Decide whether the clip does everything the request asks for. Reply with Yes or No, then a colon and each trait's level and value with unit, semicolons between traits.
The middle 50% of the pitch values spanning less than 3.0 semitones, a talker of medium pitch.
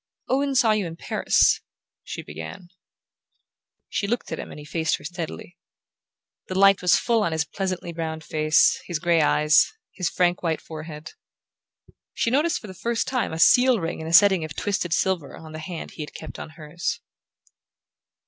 No: average, 3.8 semitones; medium, 170 Hz